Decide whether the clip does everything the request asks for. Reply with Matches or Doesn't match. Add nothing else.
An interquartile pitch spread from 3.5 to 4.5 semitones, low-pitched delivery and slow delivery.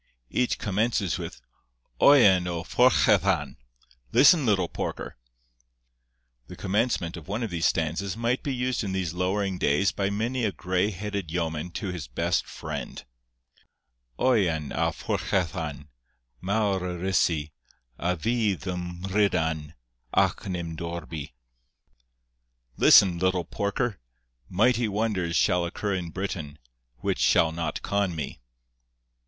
Matches